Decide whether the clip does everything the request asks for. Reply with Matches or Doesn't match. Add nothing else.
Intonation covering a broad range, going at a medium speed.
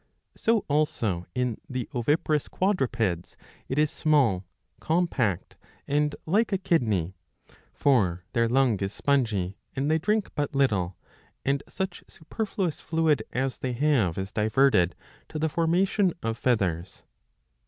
Doesn't match